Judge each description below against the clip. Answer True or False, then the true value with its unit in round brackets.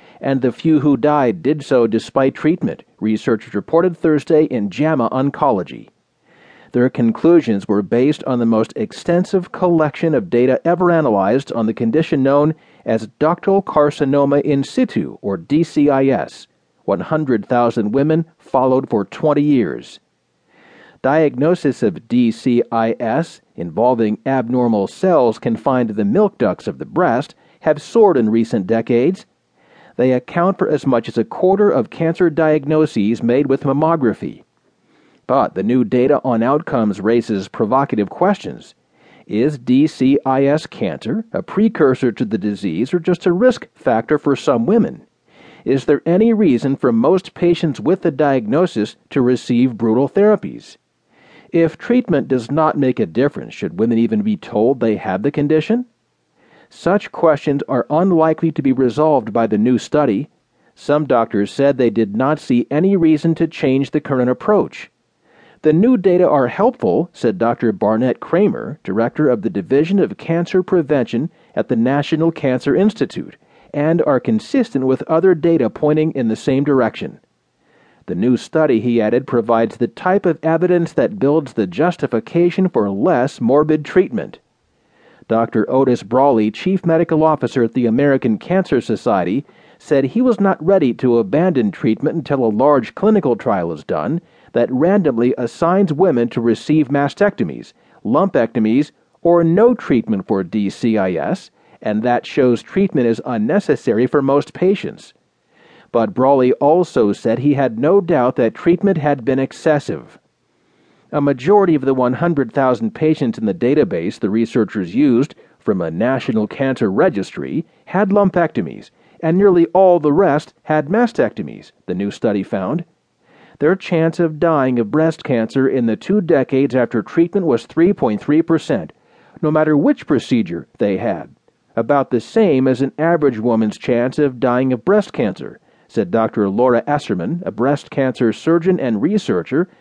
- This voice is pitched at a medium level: True (145 Hz)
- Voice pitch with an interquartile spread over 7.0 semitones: False (5.5 semitones)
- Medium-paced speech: True (145 wpm)